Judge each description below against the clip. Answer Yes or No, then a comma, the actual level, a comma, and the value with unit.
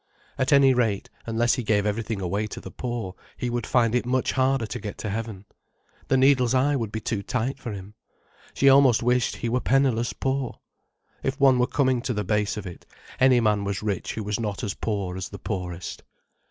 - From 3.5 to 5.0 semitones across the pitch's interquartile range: Yes, average, 3.9 semitones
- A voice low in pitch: Yes, low, 115 Hz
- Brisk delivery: Yes, fast, 210 wpm